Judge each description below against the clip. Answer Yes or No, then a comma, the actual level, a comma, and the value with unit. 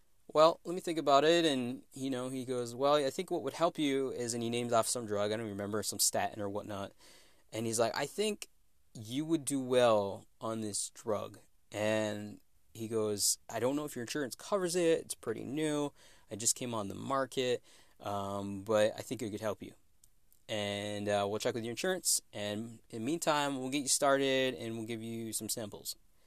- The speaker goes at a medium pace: No, fast, 215 wpm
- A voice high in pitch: No, low, 120 Hz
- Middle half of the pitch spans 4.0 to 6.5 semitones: Yes, average, 4.9 semitones